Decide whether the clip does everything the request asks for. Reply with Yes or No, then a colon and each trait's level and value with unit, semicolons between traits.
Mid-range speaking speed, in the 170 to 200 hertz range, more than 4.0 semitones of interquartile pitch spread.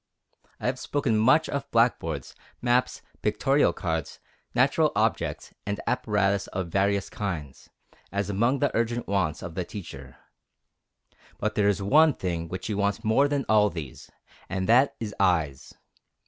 No: average, 145 wpm; low, 100 Hz; average, 4.7 semitones